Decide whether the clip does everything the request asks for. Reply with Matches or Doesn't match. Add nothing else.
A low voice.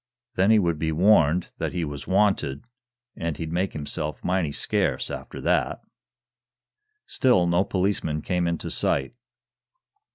Matches